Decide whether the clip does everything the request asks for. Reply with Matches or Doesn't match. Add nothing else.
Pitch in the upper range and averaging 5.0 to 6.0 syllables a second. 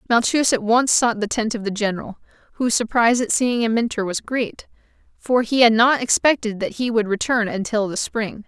Matches